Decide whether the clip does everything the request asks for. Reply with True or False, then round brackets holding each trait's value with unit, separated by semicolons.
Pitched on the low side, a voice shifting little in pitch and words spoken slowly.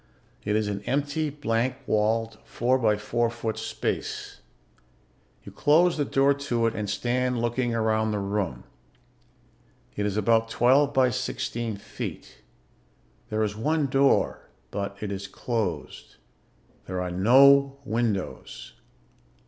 False (115 Hz; 3.9 semitones; 130 wpm)